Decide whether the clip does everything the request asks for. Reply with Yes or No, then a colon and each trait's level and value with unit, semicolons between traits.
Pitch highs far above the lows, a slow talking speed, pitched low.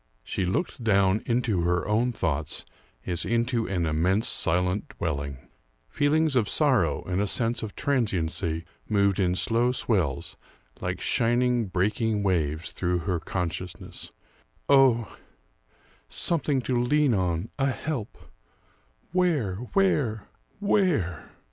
Yes: wide, 5.9 semitones; slow, 115 wpm; low, 105 Hz